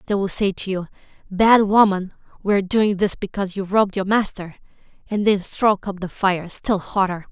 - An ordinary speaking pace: Yes, average, 195 wpm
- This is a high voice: Yes, high, 195 Hz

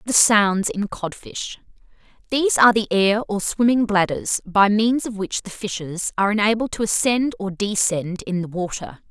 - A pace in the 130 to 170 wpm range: Yes, average, 165 wpm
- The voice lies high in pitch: Yes, high, 205 Hz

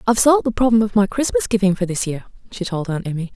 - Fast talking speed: Yes, fast, 270 wpm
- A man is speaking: No, female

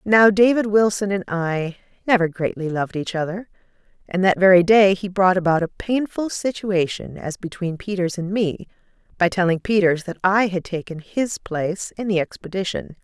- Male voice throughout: No, female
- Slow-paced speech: No, average, 170 wpm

